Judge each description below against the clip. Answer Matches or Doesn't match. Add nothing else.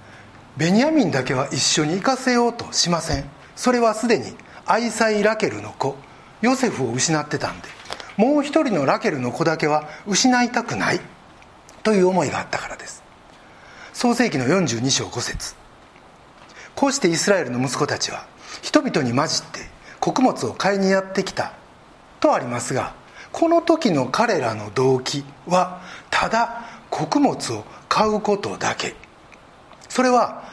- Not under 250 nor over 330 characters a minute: Matches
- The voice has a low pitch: Doesn't match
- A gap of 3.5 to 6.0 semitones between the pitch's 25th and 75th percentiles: Doesn't match